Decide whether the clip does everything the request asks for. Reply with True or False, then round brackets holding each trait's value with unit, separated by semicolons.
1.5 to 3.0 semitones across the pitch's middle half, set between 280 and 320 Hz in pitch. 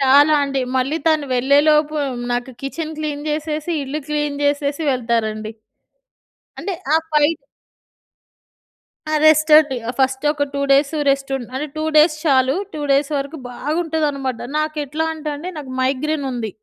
True (2.4 semitones; 290 Hz)